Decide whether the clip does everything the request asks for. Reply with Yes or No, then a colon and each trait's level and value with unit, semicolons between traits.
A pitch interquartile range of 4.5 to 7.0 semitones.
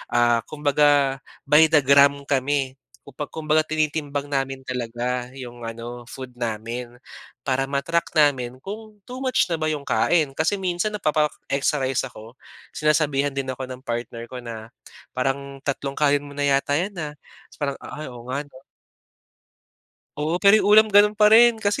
No: average, 3.2 semitones